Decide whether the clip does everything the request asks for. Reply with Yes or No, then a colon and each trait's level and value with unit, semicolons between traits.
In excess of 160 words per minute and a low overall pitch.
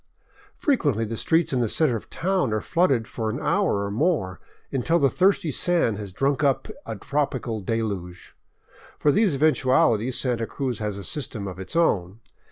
Yes: average, 175 wpm; low, 125 Hz